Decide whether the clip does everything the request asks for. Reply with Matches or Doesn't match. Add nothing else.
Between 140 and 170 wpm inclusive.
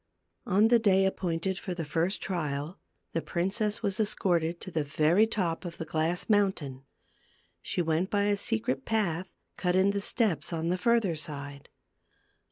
Matches